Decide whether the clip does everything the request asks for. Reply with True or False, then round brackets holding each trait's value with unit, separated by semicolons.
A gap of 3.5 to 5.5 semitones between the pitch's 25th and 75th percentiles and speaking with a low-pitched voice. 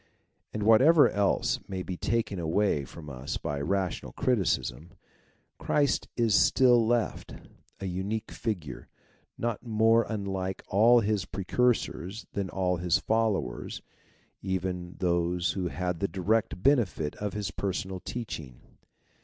True (4.0 semitones; 95 Hz)